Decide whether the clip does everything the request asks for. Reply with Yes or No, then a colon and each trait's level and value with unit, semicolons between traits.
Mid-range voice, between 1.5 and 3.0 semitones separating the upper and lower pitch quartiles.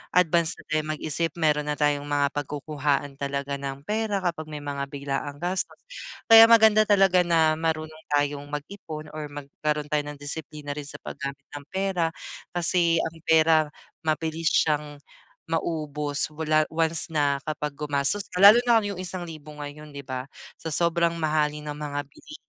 Yes: medium, 155 Hz; narrow, 2.4 semitones